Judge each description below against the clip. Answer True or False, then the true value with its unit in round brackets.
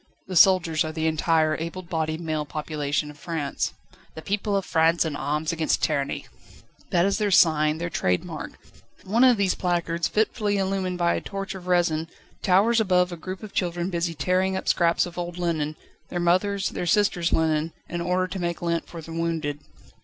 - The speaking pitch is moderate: True (170 Hz)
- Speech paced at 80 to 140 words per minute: False (190 wpm)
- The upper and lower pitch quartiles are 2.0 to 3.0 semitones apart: True (2.7 semitones)